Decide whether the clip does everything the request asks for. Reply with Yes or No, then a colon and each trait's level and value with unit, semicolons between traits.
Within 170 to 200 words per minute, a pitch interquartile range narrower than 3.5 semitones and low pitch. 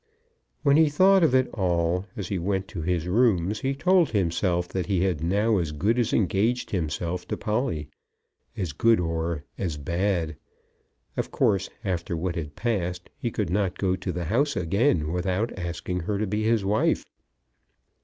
No: average, 175 wpm; average, 4.4 semitones; very low, 95 Hz